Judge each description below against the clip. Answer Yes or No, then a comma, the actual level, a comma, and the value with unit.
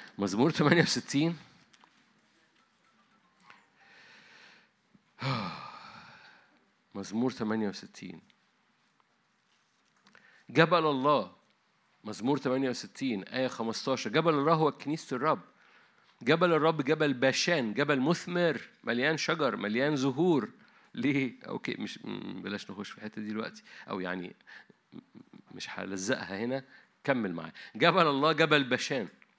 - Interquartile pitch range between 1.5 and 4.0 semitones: No, average, 4.8 semitones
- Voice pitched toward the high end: No, medium, 140 Hz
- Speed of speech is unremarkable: Yes, average, 90 wpm